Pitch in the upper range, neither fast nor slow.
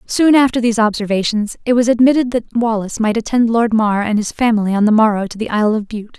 No: high, 225 Hz; fast, 235 wpm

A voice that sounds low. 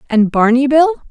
No: very high, 265 Hz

